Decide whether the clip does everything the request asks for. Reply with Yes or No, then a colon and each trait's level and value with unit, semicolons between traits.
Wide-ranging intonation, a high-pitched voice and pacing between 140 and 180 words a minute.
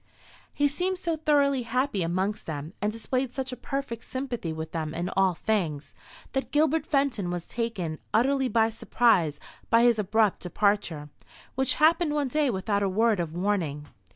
Yes: wide, 7.1 semitones; high, 225 Hz; average, 165 wpm